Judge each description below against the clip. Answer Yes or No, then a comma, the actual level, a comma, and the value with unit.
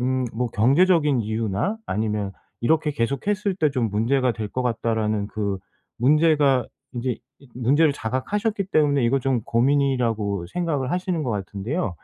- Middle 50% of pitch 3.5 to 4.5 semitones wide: No, average, 5.2 semitones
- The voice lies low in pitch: Yes, low, 130 Hz